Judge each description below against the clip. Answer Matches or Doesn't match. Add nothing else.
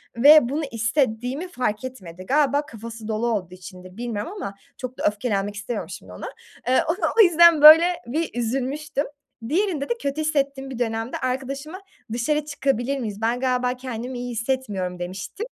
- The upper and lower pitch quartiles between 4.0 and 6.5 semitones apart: Matches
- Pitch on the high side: Matches